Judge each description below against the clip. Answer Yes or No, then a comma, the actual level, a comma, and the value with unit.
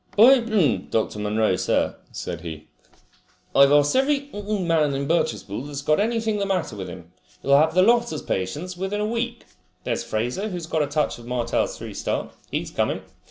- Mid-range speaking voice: Yes, medium, 155 Hz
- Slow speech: No, average, 180 wpm